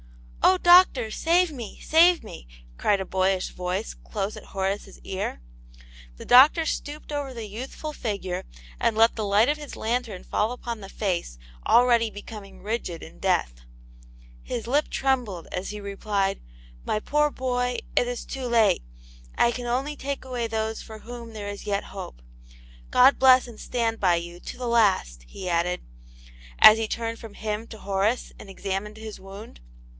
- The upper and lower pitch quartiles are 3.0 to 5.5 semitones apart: Yes, average, 4.1 semitones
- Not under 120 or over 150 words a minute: No, average, 175 wpm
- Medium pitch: No, high, 220 Hz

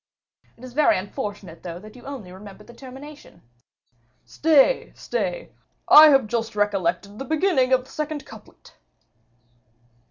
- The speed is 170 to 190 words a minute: No, slow, 135 wpm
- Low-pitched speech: No, very high, 250 Hz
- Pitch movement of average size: No, wide, 6.0 semitones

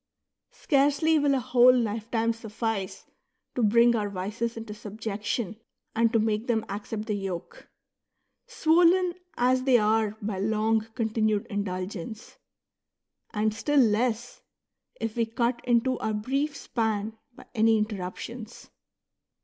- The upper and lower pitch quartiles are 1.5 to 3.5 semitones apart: Yes, narrow, 2.4 semitones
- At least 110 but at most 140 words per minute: Yes, slow, 135 wpm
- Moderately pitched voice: No, high, 225 Hz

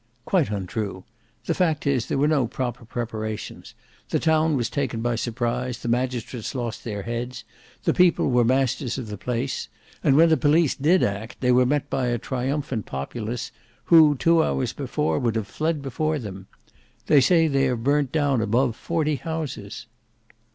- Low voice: Yes, low, 130 Hz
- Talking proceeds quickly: No, average, 170 wpm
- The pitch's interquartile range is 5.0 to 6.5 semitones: No, average, 4.1 semitones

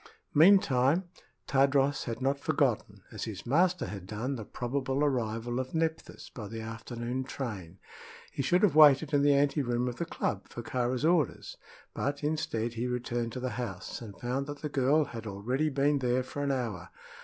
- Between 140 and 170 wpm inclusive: No, average, 180 wpm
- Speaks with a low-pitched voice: Yes, low, 130 Hz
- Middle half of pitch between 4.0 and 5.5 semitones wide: No, average, 3.3 semitones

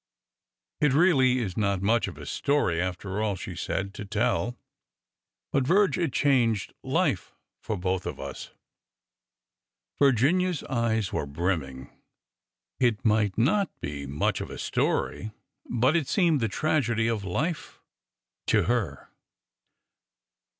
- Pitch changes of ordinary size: No, wide, 6.2 semitones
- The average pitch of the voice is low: Yes, low, 115 Hz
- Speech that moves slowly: Yes, slow, 130 wpm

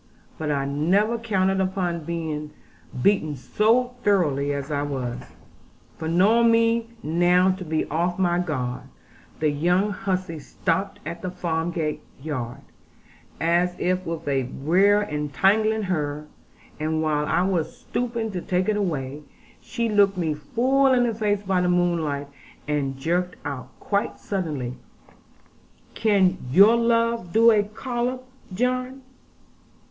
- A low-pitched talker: No, medium, 180 Hz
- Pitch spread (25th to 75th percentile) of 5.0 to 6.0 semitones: Yes, wide, 5.4 semitones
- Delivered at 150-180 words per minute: No, slow, 135 wpm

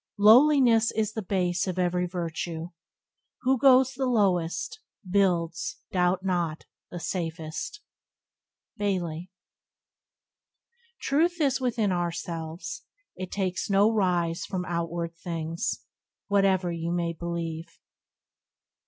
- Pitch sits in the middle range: Yes, medium, 180 Hz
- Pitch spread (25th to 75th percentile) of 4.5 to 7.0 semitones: No, average, 3.8 semitones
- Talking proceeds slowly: Yes, slow, 100 wpm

